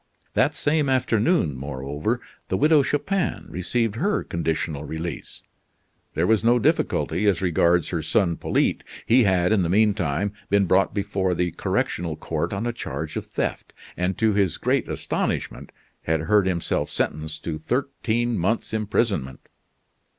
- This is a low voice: Yes, very low, 95 Hz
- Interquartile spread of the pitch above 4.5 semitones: Yes, wide, 5.6 semitones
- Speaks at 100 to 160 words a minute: Yes, average, 150 wpm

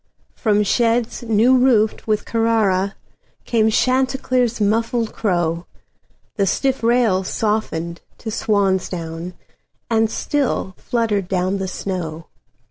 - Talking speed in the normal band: No, slow, 95 wpm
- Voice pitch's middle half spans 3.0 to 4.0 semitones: Yes, average, 3.6 semitones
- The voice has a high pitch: Yes, high, 215 Hz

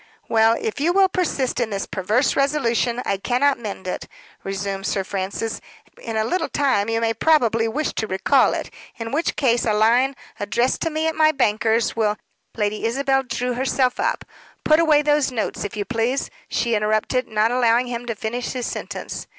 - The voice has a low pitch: No, high, 235 Hz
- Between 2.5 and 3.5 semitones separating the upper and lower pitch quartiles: No, average, 3.9 semitones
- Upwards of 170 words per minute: Yes, average, 190 wpm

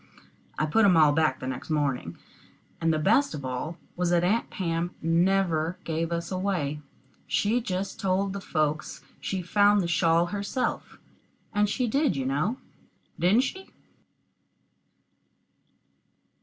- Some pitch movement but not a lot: Yes, average, 4.4 semitones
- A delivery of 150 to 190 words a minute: No, average, 140 wpm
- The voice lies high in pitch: No, medium, 175 Hz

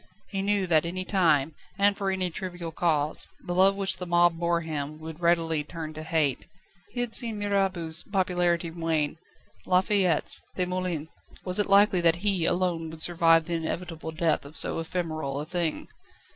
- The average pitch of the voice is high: No, medium, 170 Hz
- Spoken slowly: No, average, 175 wpm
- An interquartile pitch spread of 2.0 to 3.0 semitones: Yes, narrow, 2.5 semitones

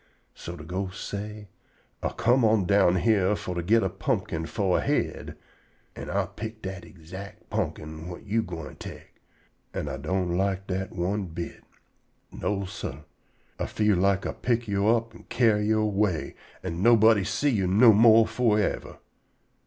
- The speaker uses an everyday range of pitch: Yes, average, 3.2 semitones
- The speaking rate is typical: Yes, average, 170 wpm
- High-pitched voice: No, low, 100 Hz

